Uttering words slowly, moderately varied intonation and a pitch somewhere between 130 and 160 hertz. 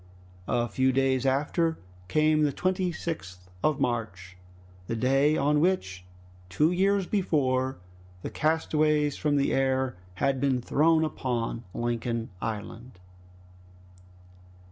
Yes: slow, 110 wpm; average, 4.5 semitones; low, 135 Hz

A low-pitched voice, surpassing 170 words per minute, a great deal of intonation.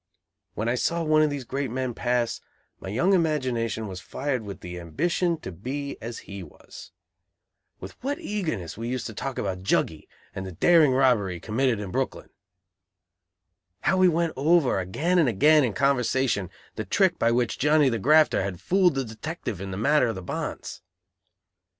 Yes: low, 125 Hz; average, 180 wpm; wide, 7.0 semitones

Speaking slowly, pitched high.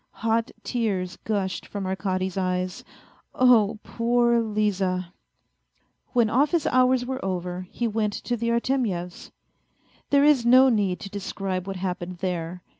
Yes: slow, 130 wpm; high, 205 Hz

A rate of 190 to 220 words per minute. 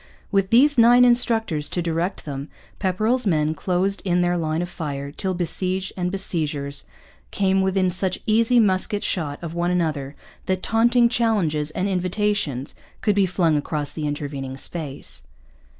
No: average, 150 wpm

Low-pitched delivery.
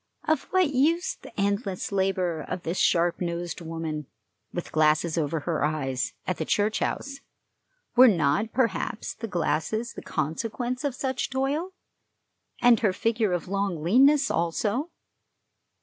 No: high, 195 Hz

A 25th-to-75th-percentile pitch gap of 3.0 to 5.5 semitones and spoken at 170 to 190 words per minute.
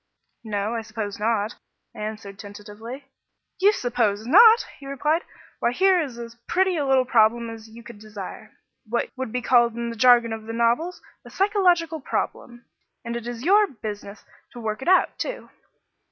Yes: average, 4.9 semitones; average, 175 wpm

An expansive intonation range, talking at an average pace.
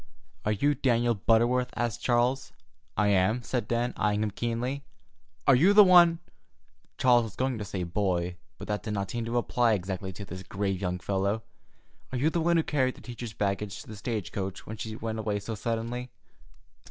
No: average, 3.7 semitones; average, 190 wpm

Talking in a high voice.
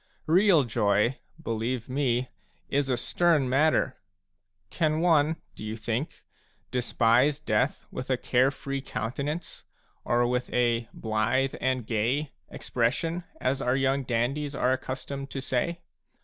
No: low, 130 Hz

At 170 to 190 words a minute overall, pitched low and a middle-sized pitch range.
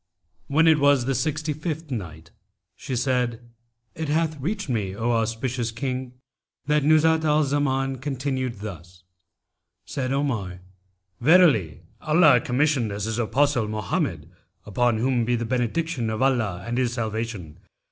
No: slow, 135 wpm; low, 125 Hz; average, 4.5 semitones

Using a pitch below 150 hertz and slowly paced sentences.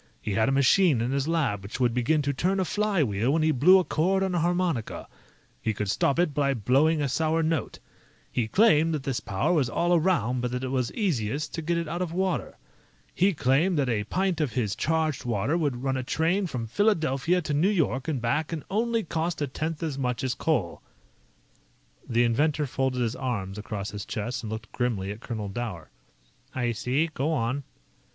No: medium, 140 Hz; fast, 205 wpm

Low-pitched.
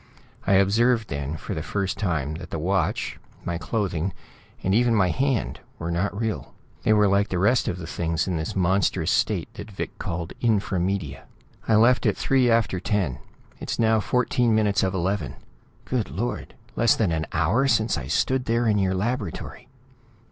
Yes: low, 100 Hz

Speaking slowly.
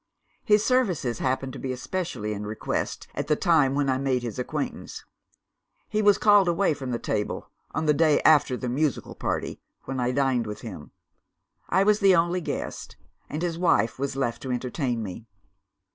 No: average, 180 wpm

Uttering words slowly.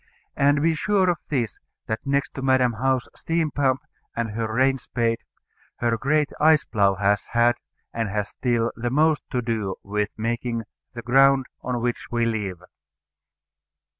No: average, 160 wpm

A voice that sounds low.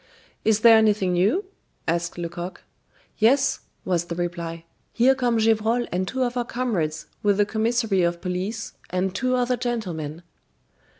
No: high, 210 Hz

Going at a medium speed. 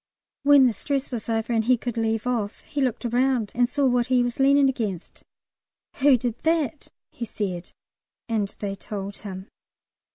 Yes: average, 170 wpm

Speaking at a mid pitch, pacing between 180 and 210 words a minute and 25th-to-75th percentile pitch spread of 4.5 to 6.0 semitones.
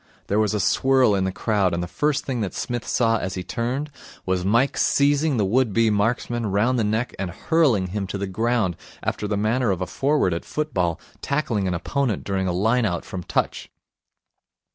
No: low, 110 Hz; fast, 205 wpm; average, 4.9 semitones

